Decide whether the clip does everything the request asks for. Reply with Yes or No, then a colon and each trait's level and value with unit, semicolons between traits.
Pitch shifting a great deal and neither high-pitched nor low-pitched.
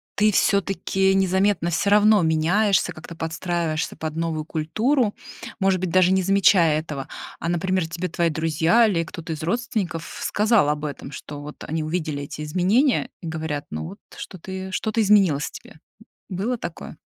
No: average, 3.7 semitones; medium, 175 Hz